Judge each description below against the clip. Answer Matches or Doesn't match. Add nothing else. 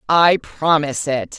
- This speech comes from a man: Doesn't match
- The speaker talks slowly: Matches